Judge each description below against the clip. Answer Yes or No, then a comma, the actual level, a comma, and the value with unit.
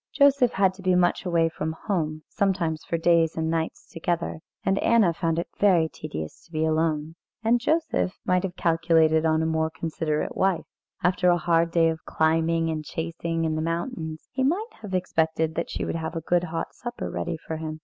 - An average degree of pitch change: No, narrow, 2.3 semitones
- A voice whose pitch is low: No, medium, 165 Hz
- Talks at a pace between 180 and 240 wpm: Yes, average, 200 wpm